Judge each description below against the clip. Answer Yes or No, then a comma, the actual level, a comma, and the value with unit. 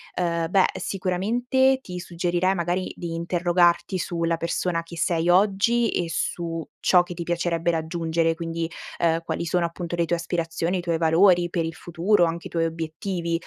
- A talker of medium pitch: Yes, medium, 170 Hz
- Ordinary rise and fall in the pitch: No, narrow, 1.5 semitones